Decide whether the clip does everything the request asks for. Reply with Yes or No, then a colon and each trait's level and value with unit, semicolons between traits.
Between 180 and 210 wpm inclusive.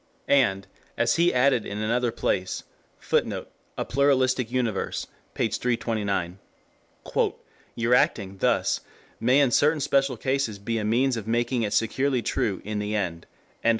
No: average, 140 wpm